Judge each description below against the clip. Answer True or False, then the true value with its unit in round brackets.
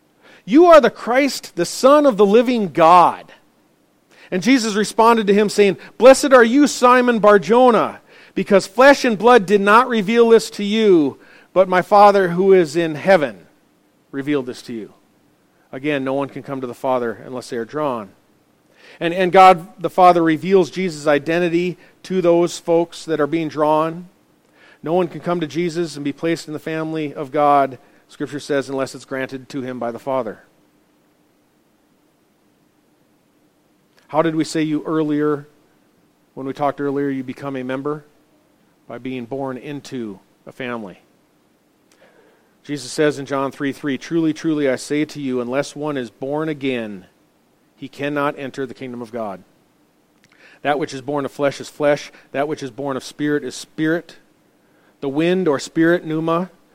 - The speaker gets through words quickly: False (170 wpm)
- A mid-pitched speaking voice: True (155 Hz)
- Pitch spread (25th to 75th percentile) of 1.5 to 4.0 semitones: False (5.2 semitones)